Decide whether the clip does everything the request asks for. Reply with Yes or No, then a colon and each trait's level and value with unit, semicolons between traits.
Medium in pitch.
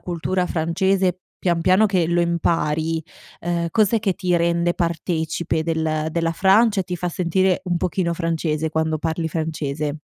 Yes: medium, 170 Hz